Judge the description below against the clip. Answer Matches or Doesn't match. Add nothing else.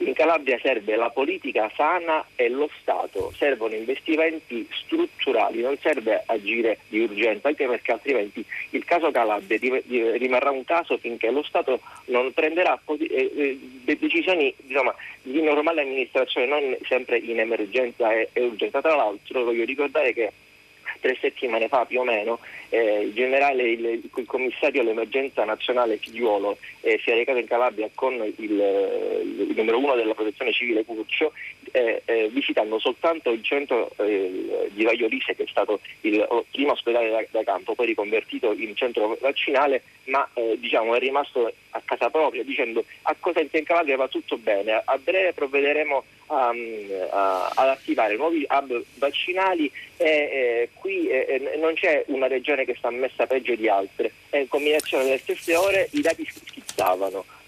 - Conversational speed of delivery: Matches